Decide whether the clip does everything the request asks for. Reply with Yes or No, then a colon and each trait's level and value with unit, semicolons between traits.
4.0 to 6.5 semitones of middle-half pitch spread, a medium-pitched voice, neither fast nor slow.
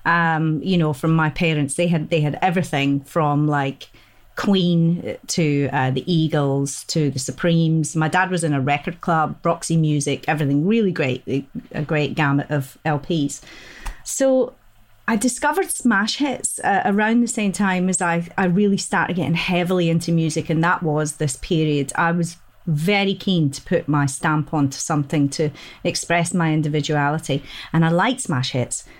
No: average, 3.6 semitones; medium, 160 Hz; average, 170 wpm